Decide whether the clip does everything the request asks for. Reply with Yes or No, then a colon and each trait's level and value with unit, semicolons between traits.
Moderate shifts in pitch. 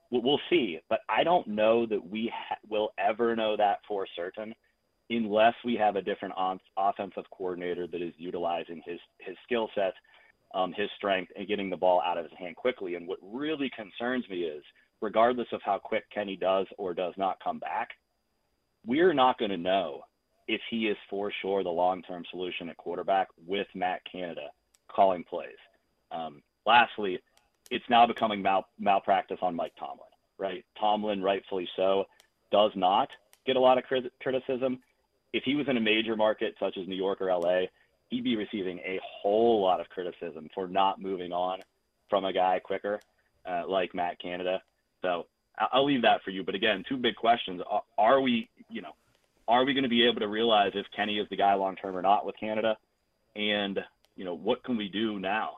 Yes: average, 3.7 semitones